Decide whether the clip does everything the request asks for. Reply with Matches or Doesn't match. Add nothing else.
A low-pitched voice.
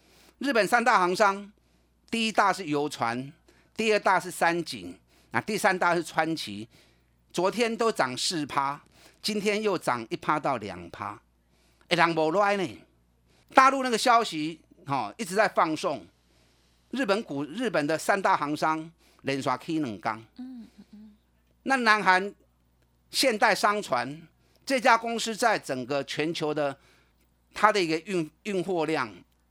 Doesn't match